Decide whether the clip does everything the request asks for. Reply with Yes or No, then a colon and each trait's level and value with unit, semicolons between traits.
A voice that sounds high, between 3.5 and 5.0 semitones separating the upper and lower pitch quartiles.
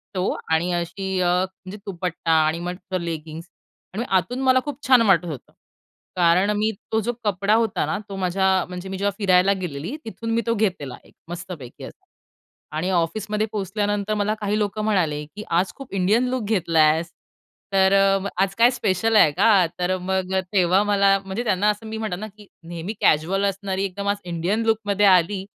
No: high, 195 Hz; average, 3.0 semitones